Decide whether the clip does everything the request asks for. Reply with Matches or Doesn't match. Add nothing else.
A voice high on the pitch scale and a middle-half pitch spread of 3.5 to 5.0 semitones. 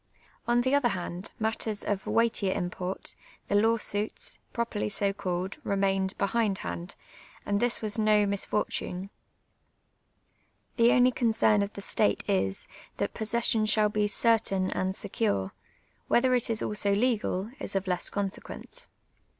Doesn't match